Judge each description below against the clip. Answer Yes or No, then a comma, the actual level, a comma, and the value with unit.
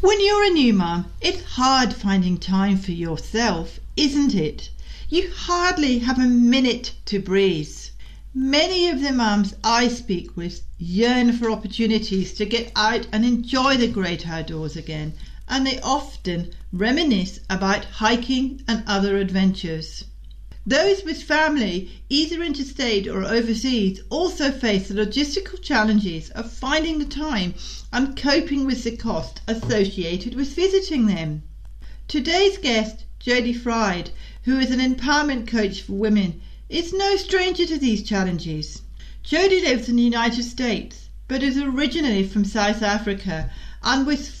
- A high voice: Yes, high, 235 Hz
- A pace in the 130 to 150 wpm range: Yes, average, 140 wpm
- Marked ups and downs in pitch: Yes, wide, 6.0 semitones